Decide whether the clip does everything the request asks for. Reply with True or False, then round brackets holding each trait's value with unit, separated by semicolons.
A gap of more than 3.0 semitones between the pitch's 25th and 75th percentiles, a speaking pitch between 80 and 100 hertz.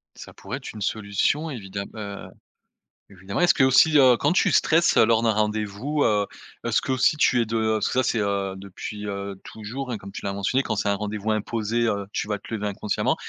False (3.4 semitones; 110 Hz)